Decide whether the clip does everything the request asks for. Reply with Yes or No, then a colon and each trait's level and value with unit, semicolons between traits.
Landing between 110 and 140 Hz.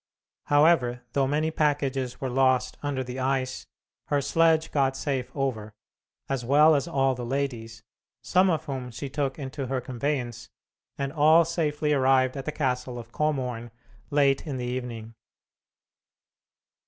Yes: low, 135 Hz